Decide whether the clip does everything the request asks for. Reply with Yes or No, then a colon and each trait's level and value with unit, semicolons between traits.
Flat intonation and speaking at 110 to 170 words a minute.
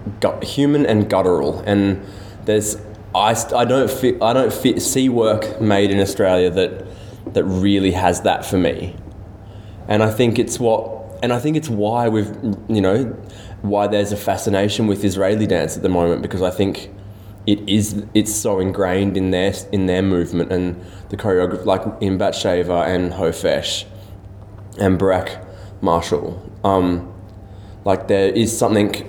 Yes: narrow, 2.0 semitones; average, 160 wpm